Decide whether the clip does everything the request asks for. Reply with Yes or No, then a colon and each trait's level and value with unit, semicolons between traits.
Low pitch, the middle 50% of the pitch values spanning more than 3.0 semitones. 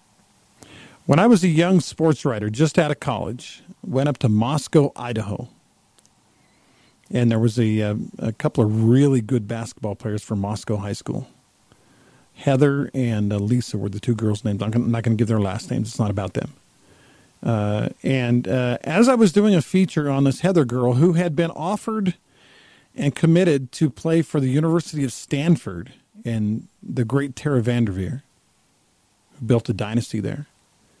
Yes: low, 125 Hz; wide, 5.6 semitones